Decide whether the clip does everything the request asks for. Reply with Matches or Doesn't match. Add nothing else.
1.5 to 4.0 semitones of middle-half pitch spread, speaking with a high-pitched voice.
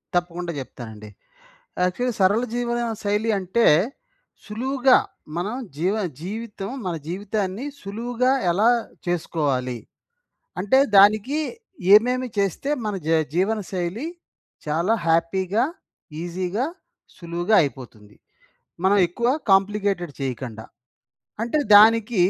Doesn't match